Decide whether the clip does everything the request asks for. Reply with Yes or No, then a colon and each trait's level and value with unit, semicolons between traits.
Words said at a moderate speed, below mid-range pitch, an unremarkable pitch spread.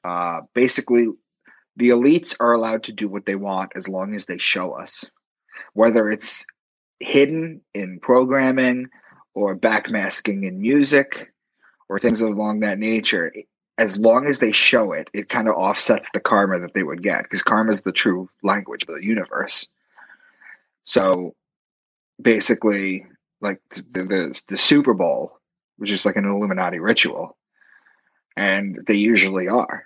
Yes: average, 150 wpm; low, 105 Hz; average, 3.8 semitones